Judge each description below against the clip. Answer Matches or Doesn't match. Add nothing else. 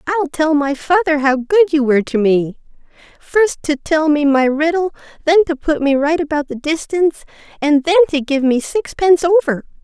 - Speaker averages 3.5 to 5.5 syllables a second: Matches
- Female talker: Matches